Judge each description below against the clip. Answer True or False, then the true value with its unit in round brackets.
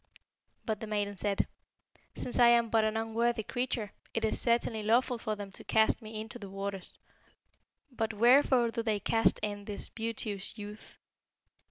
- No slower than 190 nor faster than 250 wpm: False (165 wpm)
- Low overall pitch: False (220 Hz)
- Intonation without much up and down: True (2.0 semitones)